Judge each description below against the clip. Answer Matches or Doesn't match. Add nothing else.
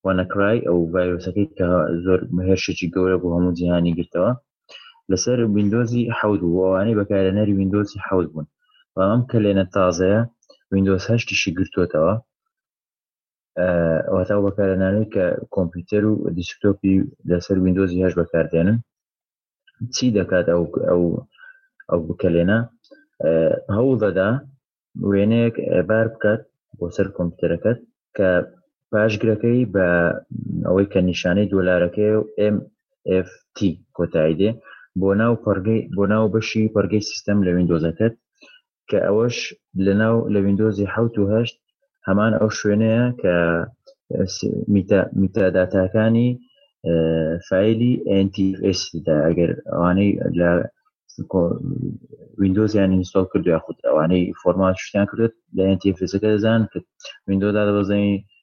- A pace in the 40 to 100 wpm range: Doesn't match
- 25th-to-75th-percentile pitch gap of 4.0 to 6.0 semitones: Doesn't match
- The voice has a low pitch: Matches